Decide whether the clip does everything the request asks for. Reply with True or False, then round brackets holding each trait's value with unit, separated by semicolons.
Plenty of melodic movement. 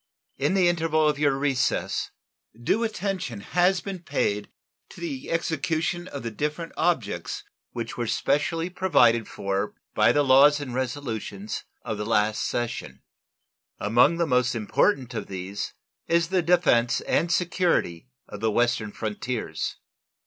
True (7.0 semitones)